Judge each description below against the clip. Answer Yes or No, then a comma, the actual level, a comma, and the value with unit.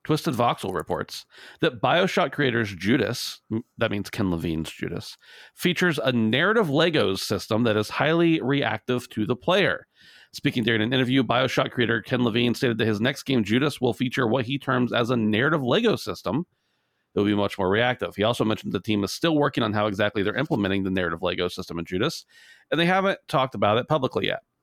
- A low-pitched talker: Yes, low, 120 Hz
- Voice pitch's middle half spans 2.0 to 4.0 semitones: No, average, 4.8 semitones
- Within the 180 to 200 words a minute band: Yes, average, 195 wpm